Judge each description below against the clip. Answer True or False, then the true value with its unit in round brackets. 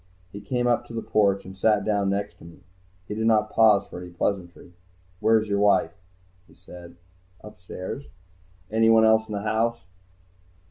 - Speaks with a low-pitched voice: True (105 Hz)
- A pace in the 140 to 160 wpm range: False (170 wpm)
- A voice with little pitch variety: True (2.3 semitones)